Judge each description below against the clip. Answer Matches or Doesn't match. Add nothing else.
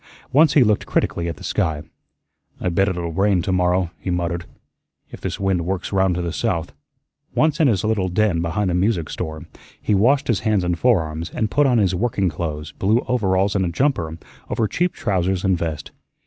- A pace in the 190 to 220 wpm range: Matches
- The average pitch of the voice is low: Matches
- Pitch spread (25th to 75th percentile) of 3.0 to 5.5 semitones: Matches